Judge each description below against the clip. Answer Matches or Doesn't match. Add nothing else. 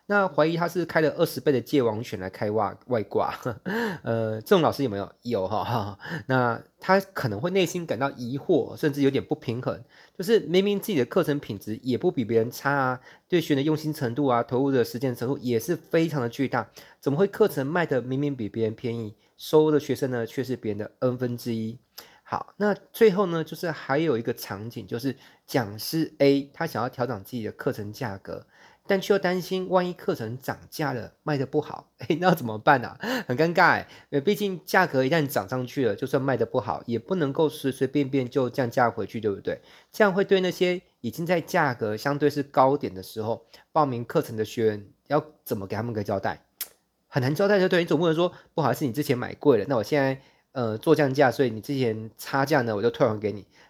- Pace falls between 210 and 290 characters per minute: Doesn't match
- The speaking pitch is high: Doesn't match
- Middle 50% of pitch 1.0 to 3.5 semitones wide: Doesn't match